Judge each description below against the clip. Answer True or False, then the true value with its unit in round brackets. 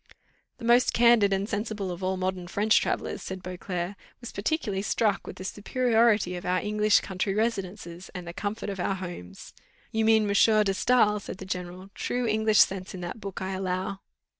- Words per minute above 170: True (190 wpm)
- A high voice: True (195 Hz)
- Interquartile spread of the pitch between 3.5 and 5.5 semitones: False (2.7 semitones)